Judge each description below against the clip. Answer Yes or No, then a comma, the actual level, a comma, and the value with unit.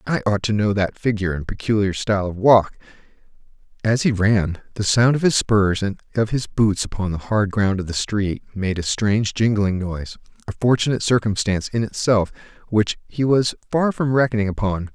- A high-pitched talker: No, low, 105 Hz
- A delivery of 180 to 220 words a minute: Yes, average, 190 wpm